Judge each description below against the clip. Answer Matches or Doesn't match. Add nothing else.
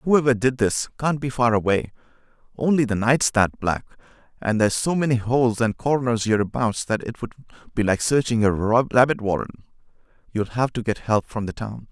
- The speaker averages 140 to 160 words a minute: Doesn't match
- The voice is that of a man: Matches